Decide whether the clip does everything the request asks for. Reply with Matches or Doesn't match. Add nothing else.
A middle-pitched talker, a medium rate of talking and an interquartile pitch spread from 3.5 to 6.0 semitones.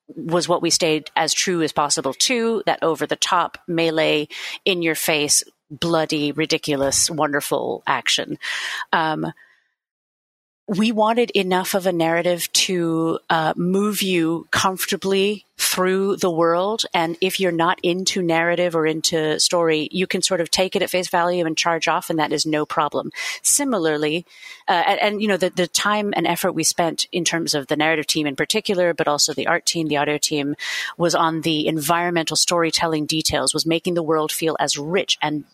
Doesn't match